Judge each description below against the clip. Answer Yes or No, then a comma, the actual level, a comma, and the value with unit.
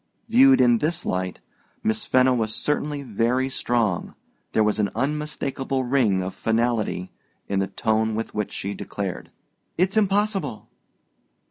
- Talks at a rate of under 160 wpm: Yes, slow, 135 wpm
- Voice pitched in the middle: No, low, 120 Hz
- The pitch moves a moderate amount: No, wide, 5.8 semitones